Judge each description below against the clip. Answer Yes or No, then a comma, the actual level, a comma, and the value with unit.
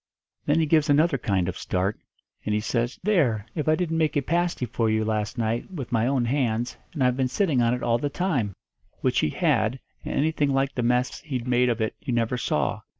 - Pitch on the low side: Yes, low, 125 Hz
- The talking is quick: Yes, fast, 225 wpm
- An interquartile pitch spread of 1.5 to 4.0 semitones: No, average, 4.4 semitones